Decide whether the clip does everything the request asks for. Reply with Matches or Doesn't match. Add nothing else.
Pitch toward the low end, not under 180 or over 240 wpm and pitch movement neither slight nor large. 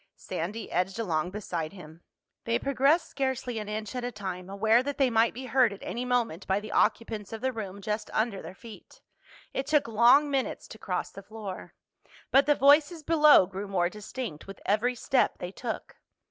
Doesn't match